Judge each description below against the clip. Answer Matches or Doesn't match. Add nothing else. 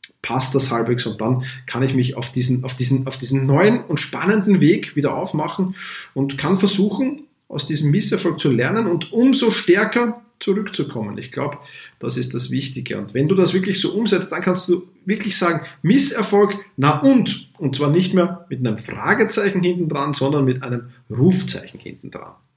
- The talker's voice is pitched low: Doesn't match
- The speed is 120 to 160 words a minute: Doesn't match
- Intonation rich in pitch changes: Matches